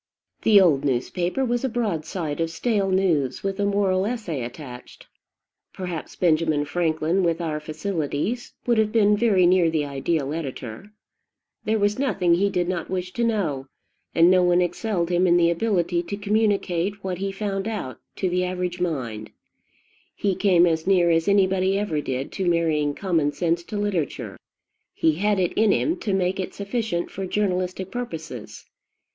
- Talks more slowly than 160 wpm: No, average, 165 wpm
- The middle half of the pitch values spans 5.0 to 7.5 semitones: No, average, 3.7 semitones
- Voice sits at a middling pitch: Yes, medium, 180 Hz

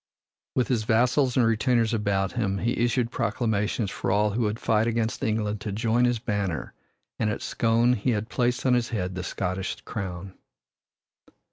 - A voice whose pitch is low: Yes, low, 110 Hz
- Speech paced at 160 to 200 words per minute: Yes, average, 170 wpm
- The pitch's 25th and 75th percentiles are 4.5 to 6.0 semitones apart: No, average, 2.7 semitones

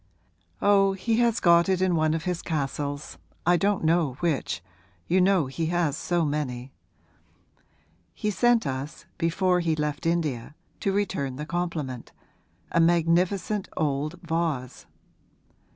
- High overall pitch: No, medium, 165 Hz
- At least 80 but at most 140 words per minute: Yes, slow, 135 wpm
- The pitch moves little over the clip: No, average, 3.7 semitones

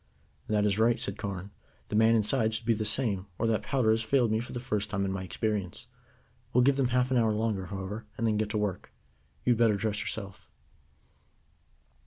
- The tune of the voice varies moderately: No, narrow, 2.2 semitones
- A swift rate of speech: Yes, fast, 215 wpm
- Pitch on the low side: Yes, low, 110 Hz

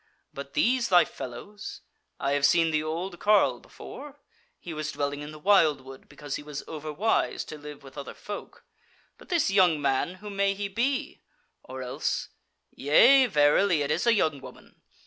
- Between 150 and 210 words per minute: Yes, average, 170 wpm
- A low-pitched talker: No, medium, 160 Hz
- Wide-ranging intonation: Yes, wide, 6.0 semitones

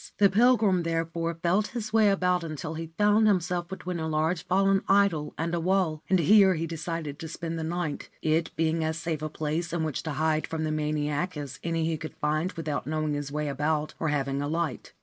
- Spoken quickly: Yes, fast, 215 wpm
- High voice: No, medium, 165 Hz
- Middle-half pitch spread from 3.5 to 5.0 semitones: No, average, 2.8 semitones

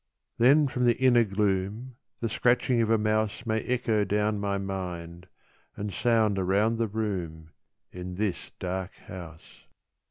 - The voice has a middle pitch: No, low, 105 Hz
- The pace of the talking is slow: No, average, 145 wpm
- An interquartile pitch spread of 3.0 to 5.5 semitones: Yes, average, 3.5 semitones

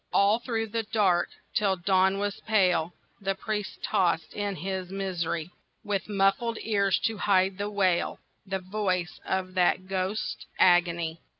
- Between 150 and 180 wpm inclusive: No, average, 140 wpm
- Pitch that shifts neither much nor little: No, narrow, 2.0 semitones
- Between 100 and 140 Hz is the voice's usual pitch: No, high, 195 Hz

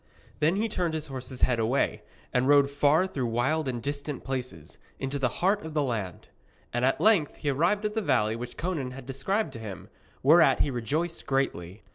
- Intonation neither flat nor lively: Yes, average, 4.5 semitones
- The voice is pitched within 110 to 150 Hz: Yes, medium, 140 Hz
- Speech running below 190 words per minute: No, average, 195 wpm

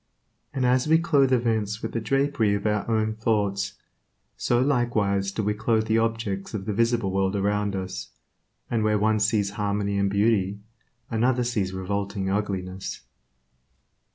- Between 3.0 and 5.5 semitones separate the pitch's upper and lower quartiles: No, narrow, 2.5 semitones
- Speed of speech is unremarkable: Yes, average, 155 wpm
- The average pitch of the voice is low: Yes, low, 105 Hz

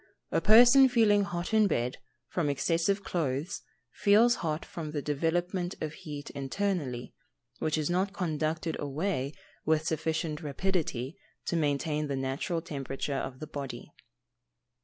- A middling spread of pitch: Yes, average, 4.3 semitones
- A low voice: No, medium, 160 Hz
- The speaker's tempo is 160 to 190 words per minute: No, slow, 135 wpm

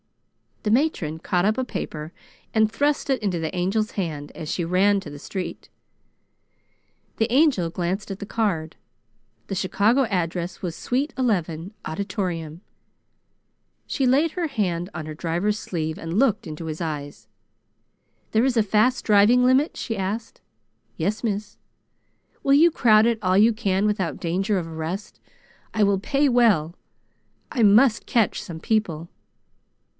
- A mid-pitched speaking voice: No, high, 200 Hz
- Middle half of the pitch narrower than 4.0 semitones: No, average, 5.2 semitones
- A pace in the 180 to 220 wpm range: No, average, 150 wpm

